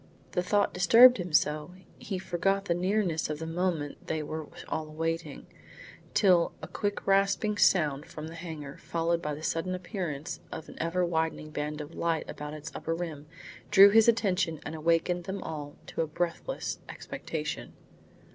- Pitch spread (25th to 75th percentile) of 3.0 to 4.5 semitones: Yes, average, 3.3 semitones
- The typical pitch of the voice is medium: Yes, medium, 165 Hz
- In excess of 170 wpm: No, average, 165 wpm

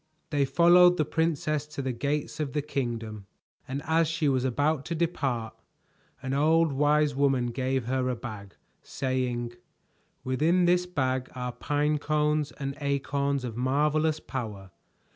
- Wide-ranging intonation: No, average, 3.1 semitones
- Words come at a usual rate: Yes, average, 145 wpm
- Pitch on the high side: No, medium, 140 Hz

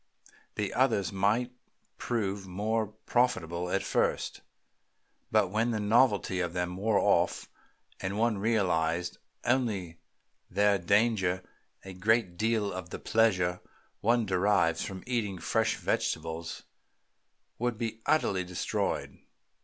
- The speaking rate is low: Yes, slow, 115 wpm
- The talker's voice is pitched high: No, low, 100 Hz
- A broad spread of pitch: No, average, 3.8 semitones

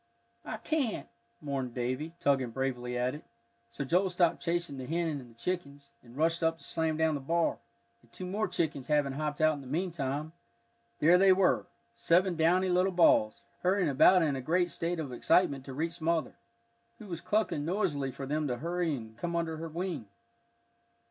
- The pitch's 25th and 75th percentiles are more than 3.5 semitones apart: Yes, average, 4.3 semitones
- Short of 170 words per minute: No, average, 190 wpm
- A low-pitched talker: No, medium, 160 Hz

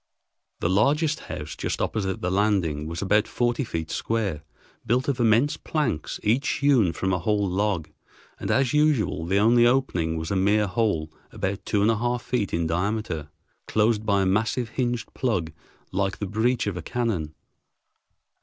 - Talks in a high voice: No, low, 105 Hz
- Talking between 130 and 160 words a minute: No, average, 170 wpm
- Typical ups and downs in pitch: Yes, average, 4.9 semitones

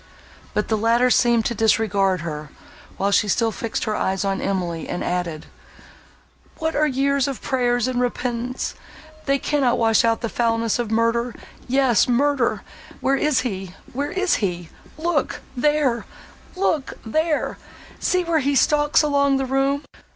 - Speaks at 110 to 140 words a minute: Yes, slow, 135 wpm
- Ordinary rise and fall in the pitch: Yes, average, 4.4 semitones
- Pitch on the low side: No, high, 245 Hz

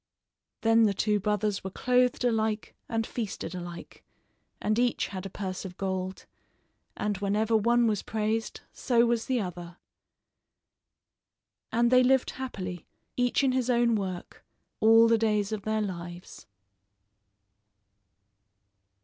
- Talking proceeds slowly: Yes, slow, 130 wpm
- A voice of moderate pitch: No, high, 215 Hz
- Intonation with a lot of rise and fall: No, average, 3.5 semitones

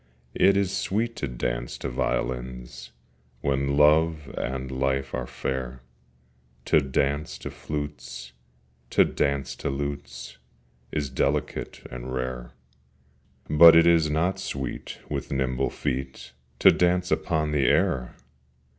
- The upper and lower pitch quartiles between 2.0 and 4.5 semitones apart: Yes, average, 3.1 semitones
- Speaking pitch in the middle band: No, very low, 70 Hz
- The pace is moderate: No, slow, 120 wpm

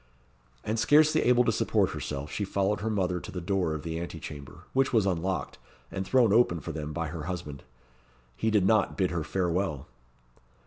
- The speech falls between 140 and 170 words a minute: No, average, 190 wpm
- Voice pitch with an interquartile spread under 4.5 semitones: No, average, 4.8 semitones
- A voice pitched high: No, very low, 95 Hz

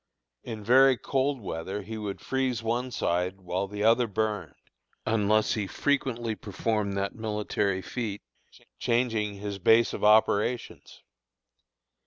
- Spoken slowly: Yes, slow, 125 wpm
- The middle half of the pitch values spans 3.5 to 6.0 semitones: No, average, 2.8 semitones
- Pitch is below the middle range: Yes, low, 110 Hz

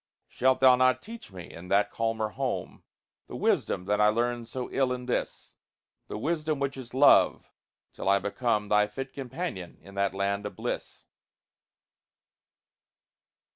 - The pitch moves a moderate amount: Yes, average, 4.3 semitones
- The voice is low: Yes, low, 115 Hz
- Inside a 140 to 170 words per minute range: Yes, average, 150 wpm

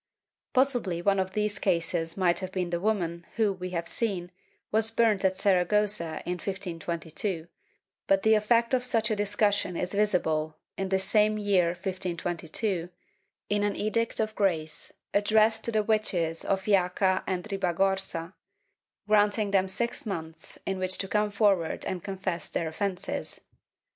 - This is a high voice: Yes, high, 195 Hz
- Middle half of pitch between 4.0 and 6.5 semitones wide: No, average, 3.0 semitones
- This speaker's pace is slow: No, average, 155 wpm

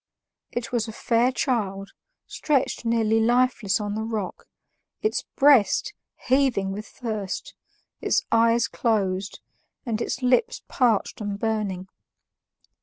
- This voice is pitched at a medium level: No, high, 225 Hz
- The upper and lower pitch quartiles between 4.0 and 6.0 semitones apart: No, average, 3.3 semitones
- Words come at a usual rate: No, slow, 115 wpm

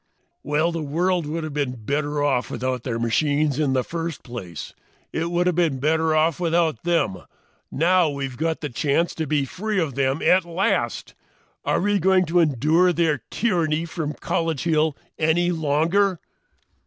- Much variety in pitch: No, average, 3.1 semitones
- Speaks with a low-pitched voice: No, medium, 160 Hz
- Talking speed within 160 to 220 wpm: Yes, average, 165 wpm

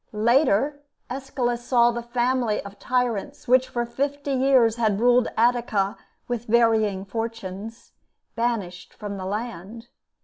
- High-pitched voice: Yes, high, 235 Hz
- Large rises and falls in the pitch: No, average, 2.8 semitones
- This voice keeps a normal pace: No, slow, 125 wpm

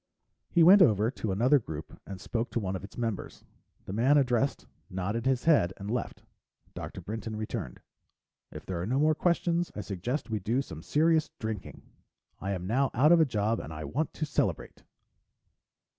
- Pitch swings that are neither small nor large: No, wide, 6.4 semitones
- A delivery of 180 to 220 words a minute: Yes, average, 185 wpm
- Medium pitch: No, low, 115 Hz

